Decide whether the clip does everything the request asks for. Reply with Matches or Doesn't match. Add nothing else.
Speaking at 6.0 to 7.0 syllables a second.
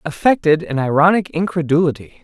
Doesn't match